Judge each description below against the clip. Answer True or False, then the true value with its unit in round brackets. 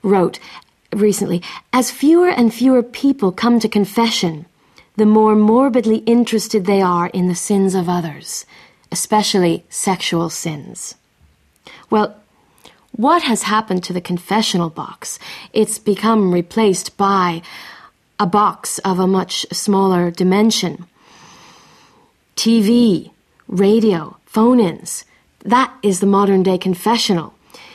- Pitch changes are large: False (3.7 semitones)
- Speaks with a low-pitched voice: False (200 Hz)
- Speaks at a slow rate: True (115 wpm)